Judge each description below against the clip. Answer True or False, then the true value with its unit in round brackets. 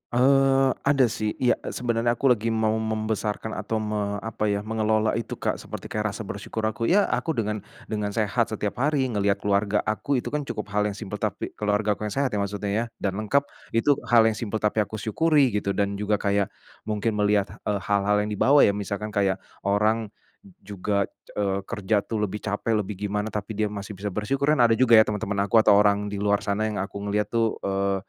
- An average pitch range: False (1.8 semitones)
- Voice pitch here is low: True (105 Hz)